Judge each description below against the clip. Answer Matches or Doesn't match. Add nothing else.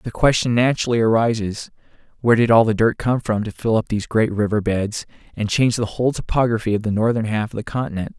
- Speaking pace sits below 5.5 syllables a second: Doesn't match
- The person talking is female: Doesn't match